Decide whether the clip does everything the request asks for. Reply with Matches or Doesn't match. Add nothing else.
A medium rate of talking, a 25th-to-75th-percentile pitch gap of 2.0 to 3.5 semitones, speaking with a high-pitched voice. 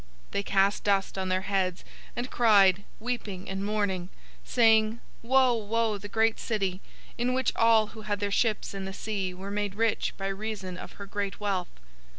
Matches